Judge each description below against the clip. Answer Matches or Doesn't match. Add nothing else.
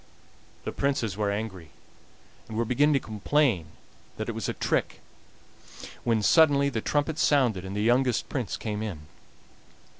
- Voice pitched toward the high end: Doesn't match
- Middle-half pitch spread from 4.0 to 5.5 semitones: Matches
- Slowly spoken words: Doesn't match